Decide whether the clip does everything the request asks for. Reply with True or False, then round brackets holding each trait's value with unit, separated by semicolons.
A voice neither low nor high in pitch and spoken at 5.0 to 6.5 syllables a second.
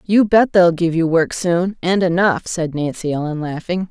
False (175 Hz; 4.5 syllables/s)